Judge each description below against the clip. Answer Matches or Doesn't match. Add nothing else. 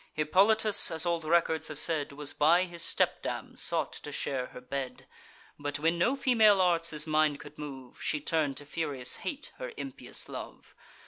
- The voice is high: Doesn't match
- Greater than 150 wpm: Matches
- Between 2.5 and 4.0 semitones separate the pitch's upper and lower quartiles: Matches